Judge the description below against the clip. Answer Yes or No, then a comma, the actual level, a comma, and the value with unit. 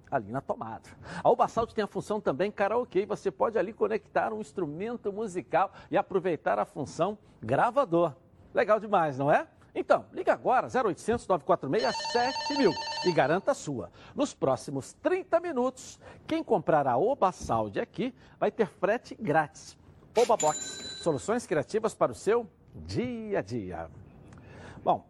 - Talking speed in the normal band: Yes, average, 150 wpm